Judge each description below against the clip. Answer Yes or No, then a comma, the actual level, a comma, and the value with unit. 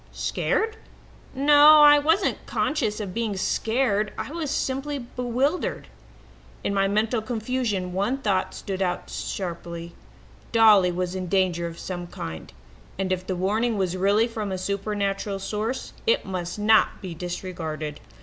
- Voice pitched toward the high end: Yes, high, 200 Hz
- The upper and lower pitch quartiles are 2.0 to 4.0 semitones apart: No, average, 4.8 semitones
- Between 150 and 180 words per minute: No, average, 140 wpm